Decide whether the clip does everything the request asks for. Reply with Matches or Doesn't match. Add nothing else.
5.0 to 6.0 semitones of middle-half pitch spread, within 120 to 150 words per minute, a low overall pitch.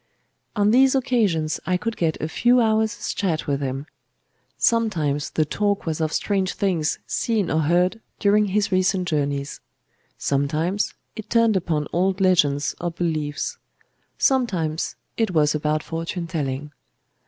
Doesn't match